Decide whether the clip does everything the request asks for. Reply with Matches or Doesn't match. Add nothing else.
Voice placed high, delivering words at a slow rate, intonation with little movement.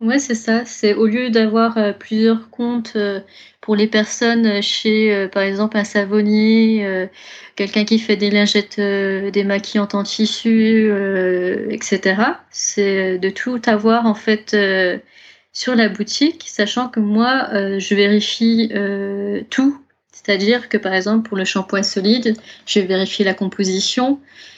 Matches